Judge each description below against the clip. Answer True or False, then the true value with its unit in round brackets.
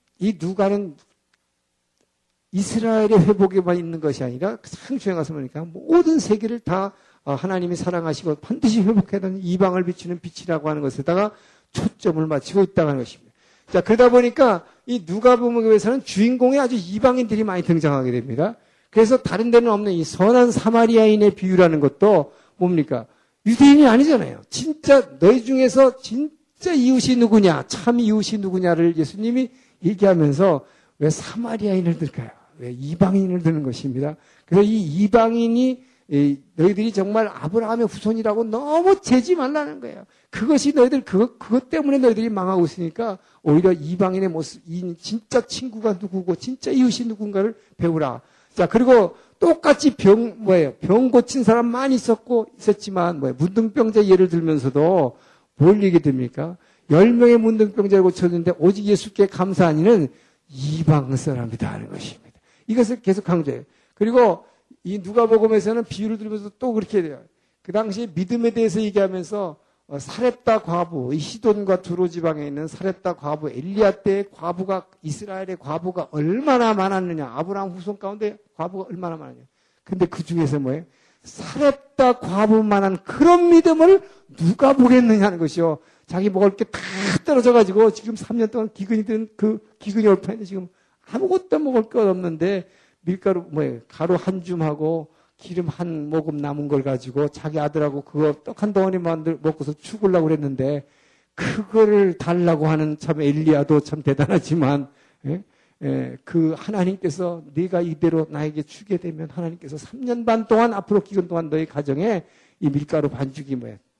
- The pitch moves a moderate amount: False (5.7 semitones)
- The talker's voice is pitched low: False (190 Hz)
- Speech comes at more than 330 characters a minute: True (350 characters per minute)